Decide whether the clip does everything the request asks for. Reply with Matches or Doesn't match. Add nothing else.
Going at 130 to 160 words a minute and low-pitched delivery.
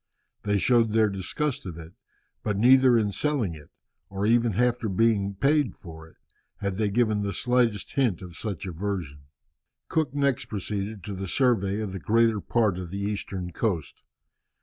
Doesn't match